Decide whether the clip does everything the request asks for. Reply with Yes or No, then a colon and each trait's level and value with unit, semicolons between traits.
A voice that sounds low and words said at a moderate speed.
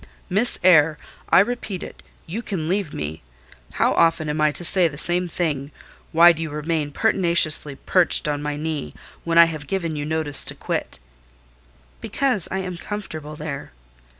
No: medium, 160 Hz; average, 170 wpm